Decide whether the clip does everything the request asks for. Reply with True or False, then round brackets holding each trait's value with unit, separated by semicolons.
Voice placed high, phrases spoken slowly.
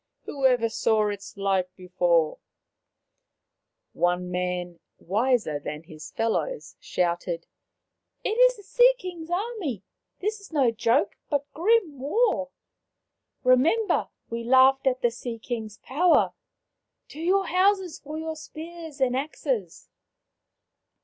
True (260 Hz; 125 wpm)